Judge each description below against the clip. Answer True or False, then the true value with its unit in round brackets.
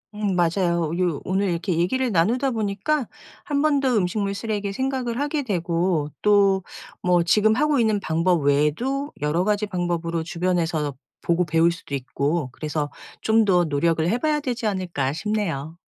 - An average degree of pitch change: True (4.7 semitones)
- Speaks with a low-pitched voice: False (185 Hz)